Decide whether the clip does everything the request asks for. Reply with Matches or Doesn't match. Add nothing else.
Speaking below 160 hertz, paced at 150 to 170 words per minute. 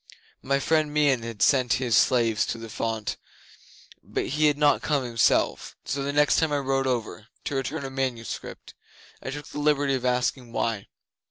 Doesn't match